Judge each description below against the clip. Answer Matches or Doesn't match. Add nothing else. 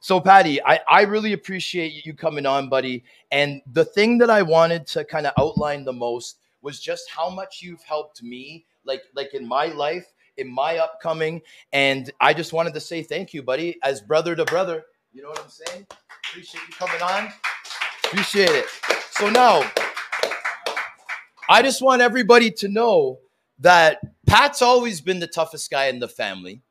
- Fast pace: Doesn't match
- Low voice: Doesn't match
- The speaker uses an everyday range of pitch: Doesn't match